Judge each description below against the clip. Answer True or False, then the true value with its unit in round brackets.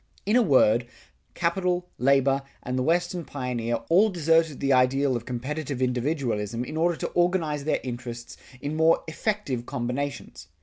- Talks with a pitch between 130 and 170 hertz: True (140 Hz)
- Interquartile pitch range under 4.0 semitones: False (4.7 semitones)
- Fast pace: False (145 wpm)